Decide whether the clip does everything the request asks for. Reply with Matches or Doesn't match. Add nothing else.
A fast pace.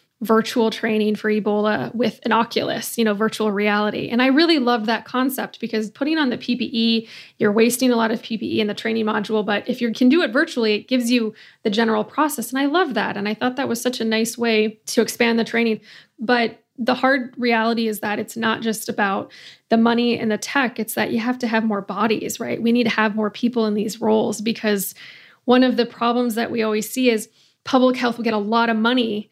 Matches